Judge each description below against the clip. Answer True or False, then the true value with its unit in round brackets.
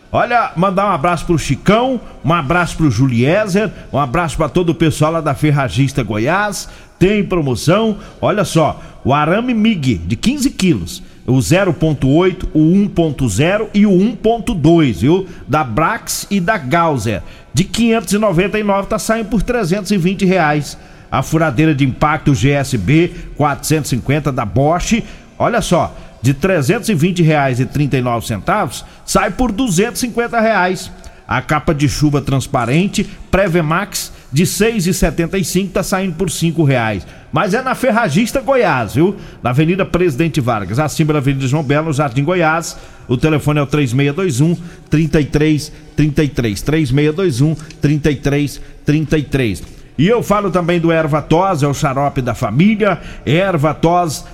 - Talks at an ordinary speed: True (135 wpm)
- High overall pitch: False (165 Hz)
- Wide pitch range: False (4.8 semitones)